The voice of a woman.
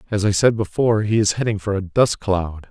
No: male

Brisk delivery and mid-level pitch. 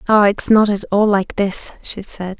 No: fast, 225 wpm; high, 200 Hz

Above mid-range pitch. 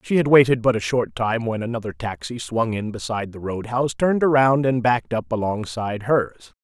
No: low, 115 Hz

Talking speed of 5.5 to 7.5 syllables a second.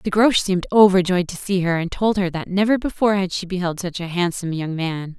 Yes: 5.9 syllables/s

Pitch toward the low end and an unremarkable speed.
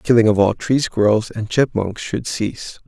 No: low, 110 Hz; fast, 210 wpm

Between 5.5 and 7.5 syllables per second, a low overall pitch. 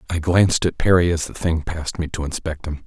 Yes: 6.0 syllables/s; very low, 85 Hz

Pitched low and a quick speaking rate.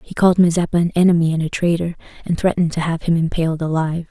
No: medium, 165 Hz; fast, 220 wpm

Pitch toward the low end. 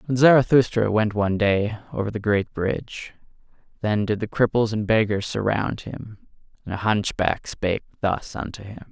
Yes: low, 105 Hz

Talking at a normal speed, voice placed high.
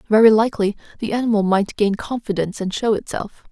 Yes: average, 170 wpm; high, 210 Hz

